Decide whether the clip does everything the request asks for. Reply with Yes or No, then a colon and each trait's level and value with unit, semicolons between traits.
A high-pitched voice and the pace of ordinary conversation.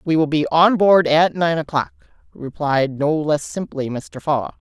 No: medium, 155 Hz; average, 180 wpm